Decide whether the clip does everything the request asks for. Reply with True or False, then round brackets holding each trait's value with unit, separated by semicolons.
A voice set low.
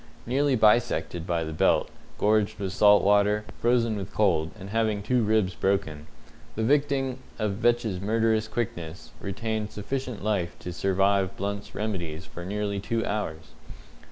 True (105 Hz)